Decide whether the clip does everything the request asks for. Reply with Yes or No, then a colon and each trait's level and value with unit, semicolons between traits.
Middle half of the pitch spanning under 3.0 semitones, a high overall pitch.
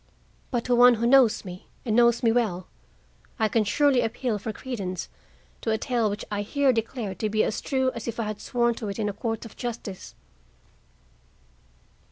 Yes: narrow, 2.6 semitones; high, 225 Hz